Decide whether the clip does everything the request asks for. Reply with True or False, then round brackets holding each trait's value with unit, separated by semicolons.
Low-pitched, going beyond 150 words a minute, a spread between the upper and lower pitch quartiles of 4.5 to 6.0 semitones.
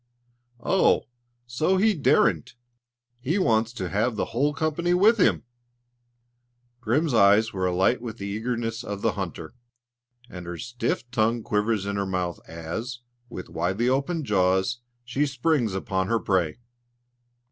False (115 Hz; 140 wpm; 5.2 semitones)